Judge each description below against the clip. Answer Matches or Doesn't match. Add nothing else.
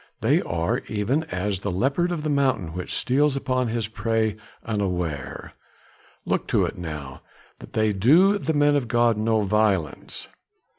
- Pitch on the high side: Doesn't match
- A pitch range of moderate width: Doesn't match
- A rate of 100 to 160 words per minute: Matches